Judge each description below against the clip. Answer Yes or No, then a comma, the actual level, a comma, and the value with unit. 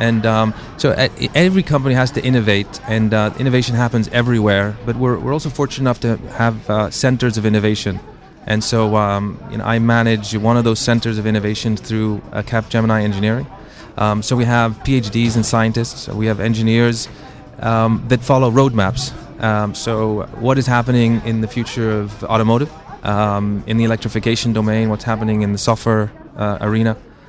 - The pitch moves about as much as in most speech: No, narrow, 2.2 semitones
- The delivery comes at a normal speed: No, fast, 180 wpm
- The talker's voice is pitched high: No, low, 115 Hz